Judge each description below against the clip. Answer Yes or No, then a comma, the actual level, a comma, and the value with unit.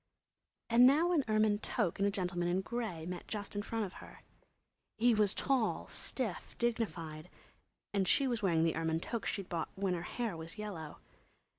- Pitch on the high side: Yes, high, 200 Hz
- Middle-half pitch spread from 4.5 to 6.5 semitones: Yes, average, 4.9 semitones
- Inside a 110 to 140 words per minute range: No, average, 180 wpm